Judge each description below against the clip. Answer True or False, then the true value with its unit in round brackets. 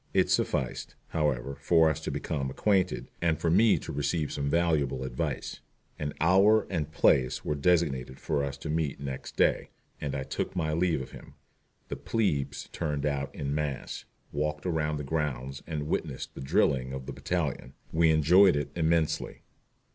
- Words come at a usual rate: True (170 wpm)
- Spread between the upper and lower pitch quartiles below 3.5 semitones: True (3.0 semitones)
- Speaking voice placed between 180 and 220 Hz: False (75 Hz)